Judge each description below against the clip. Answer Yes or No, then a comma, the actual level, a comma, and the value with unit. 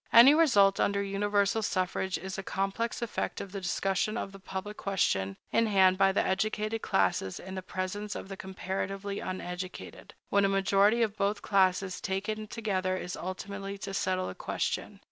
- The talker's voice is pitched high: Yes, high, 195 Hz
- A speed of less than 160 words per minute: No, average, 170 wpm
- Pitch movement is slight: Yes, narrow, 1.6 semitones